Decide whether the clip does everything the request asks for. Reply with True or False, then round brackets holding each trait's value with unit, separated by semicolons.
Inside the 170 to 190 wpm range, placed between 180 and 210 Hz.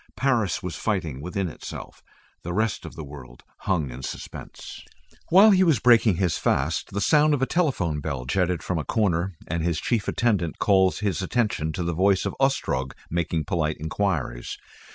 False (175 wpm; 90 Hz)